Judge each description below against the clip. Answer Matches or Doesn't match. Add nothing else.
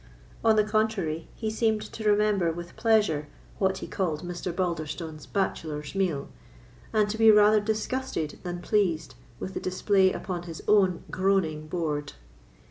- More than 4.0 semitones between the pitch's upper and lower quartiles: Matches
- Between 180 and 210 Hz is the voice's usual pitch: Matches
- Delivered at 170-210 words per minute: Doesn't match